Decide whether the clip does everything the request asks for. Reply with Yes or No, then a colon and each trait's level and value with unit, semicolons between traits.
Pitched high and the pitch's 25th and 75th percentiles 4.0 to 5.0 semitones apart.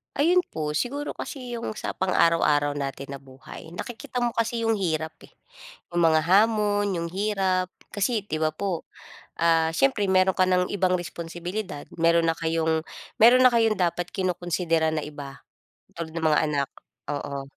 No: medium, 175 Hz; average, 4.7 semitones